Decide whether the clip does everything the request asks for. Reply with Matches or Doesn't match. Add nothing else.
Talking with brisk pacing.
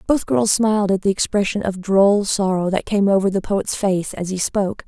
Matches